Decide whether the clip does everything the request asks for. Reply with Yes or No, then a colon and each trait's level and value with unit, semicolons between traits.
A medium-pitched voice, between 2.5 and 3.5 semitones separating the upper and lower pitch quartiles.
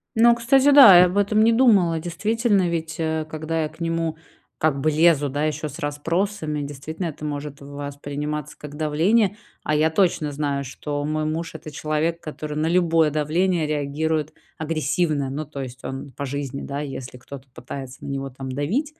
Yes: medium, 155 Hz; average, 2.9 semitones